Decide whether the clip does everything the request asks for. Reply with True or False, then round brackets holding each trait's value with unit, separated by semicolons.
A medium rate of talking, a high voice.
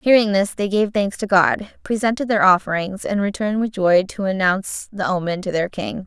False (210 wpm; 200 Hz)